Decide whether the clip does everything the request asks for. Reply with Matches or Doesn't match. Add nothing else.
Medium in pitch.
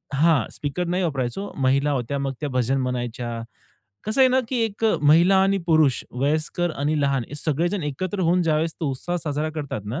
Matches